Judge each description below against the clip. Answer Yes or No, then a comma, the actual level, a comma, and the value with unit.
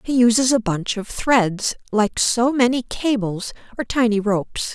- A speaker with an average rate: Yes, average, 165 wpm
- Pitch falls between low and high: No, high, 230 Hz